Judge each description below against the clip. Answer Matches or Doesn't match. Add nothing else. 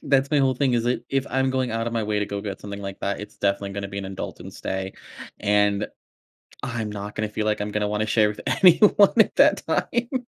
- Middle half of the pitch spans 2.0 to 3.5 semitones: Doesn't match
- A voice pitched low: Matches